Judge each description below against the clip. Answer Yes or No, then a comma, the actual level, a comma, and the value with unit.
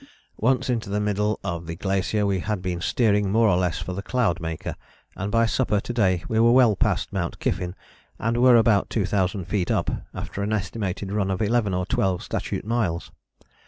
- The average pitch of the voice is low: Yes, low, 100 Hz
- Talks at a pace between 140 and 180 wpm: No, average, 190 wpm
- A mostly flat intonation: No, average, 3.5 semitones